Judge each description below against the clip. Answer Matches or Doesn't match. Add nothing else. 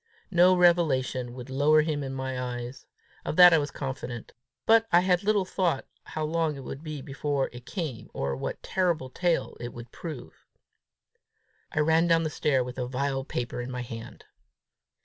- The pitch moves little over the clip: Doesn't match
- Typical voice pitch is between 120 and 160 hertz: Matches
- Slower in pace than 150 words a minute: Doesn't match